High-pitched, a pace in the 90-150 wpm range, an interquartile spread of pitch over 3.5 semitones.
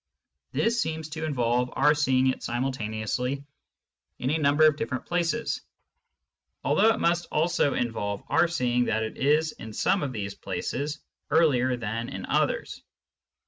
No: low, 135 Hz; average, 145 wpm; average, 4.8 semitones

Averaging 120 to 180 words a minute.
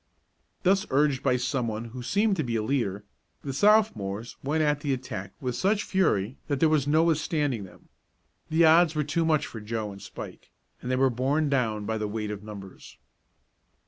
No: average, 190 wpm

